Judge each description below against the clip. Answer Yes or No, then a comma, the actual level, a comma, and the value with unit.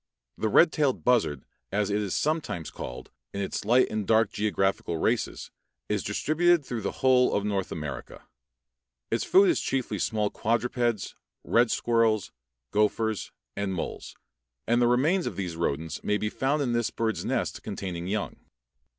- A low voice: Yes, low, 110 Hz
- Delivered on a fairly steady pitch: No, average, 4.0 semitones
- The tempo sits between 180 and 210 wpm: No, average, 160 wpm